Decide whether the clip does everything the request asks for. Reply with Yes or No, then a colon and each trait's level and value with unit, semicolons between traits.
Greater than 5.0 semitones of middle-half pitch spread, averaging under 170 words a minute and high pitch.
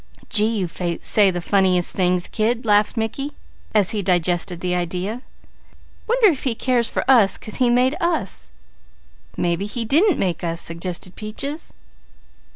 Yes: wide, 5.4 semitones; average, 150 wpm; high, 205 Hz